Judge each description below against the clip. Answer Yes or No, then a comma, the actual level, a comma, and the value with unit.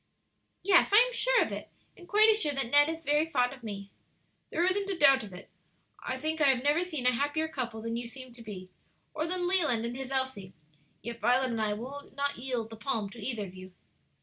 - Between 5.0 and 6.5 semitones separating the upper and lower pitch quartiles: Yes, wide, 5.6 semitones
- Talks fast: Yes, fast, 235 wpm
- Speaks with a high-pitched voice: Yes, very high, 265 Hz